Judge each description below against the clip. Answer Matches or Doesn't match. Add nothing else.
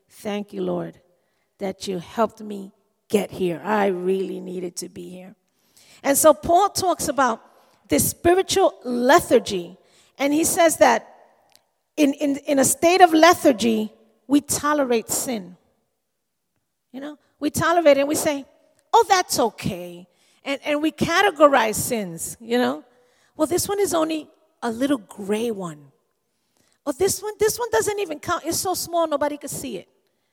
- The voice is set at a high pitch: Matches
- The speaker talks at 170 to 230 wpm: Doesn't match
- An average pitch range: Doesn't match